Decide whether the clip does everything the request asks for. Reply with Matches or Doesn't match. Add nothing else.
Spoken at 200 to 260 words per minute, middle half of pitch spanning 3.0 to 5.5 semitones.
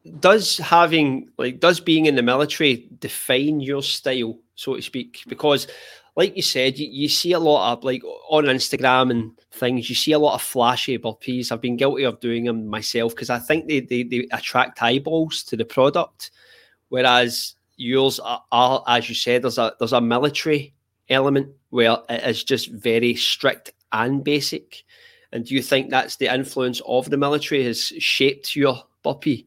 Doesn't match